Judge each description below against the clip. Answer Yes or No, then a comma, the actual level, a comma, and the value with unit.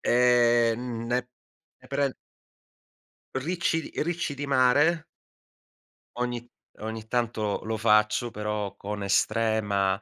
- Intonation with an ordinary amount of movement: Yes, average, 3.3 semitones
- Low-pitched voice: Yes, low, 120 Hz